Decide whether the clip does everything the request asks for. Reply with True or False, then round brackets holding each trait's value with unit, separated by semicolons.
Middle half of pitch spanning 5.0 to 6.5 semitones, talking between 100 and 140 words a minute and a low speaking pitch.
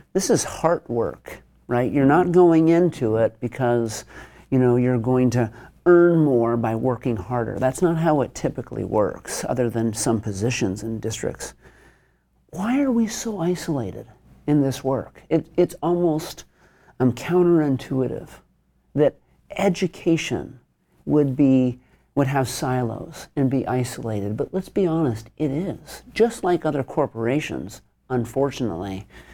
True (5.6 semitones; 135 wpm; 130 Hz)